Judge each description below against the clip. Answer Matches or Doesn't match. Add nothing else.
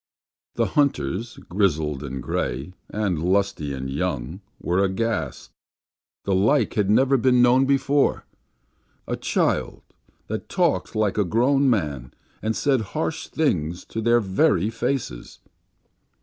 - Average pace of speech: Doesn't match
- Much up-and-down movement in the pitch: Matches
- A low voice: Matches